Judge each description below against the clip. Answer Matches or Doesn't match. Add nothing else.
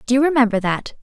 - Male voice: Doesn't match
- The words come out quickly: Matches